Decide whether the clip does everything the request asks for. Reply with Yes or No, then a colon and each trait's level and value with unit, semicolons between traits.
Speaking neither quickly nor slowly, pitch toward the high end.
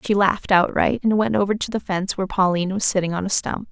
No: fast, 260 wpm; high, 195 Hz